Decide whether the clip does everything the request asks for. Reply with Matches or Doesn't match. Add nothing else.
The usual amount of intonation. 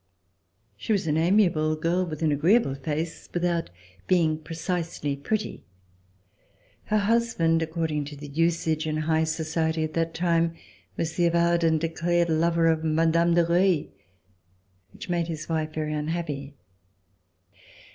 Doesn't match